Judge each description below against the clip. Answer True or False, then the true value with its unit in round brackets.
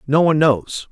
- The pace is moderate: True (195 wpm)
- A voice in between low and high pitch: True (145 Hz)